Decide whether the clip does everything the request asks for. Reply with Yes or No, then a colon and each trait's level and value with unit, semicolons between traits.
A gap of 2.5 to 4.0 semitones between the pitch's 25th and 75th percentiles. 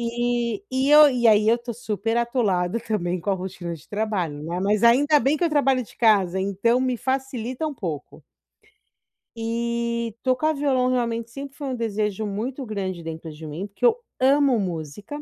No: average, 4.6 semitones